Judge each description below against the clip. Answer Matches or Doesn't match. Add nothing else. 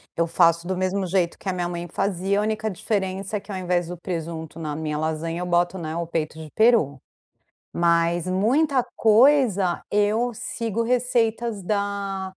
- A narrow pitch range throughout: Doesn't match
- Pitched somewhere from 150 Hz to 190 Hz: Matches